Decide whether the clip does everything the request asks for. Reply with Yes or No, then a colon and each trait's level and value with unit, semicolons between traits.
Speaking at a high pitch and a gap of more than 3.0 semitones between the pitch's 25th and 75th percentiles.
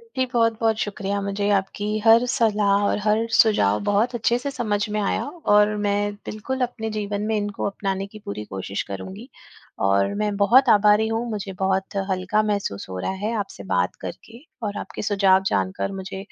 No: high, 205 Hz; narrow, 2.4 semitones